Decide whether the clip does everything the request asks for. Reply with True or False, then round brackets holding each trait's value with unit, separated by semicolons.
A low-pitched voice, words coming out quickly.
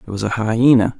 True (110 Hz; 240 wpm)